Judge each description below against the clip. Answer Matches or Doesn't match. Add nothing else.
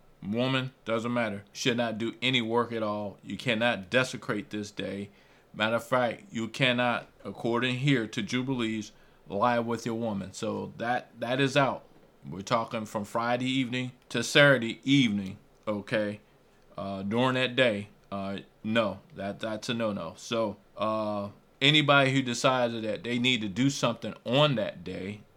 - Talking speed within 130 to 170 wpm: Matches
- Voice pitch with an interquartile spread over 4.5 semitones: Doesn't match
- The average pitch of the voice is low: Matches